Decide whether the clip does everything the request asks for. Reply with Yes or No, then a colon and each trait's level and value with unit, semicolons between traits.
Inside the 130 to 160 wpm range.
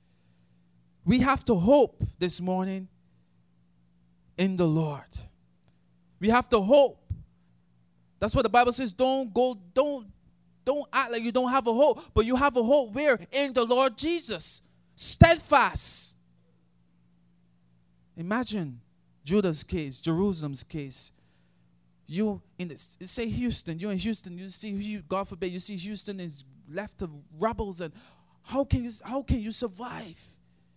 Yes: average, 140 wpm